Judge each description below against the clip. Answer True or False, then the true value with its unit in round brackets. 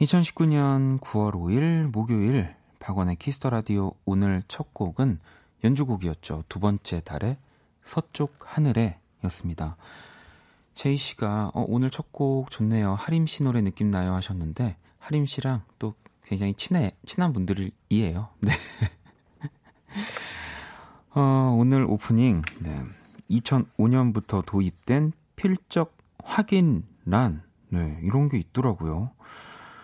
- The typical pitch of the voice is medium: False (115 Hz)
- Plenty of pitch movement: True (6.5 semitones)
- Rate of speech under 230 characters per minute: True (220 characters per minute)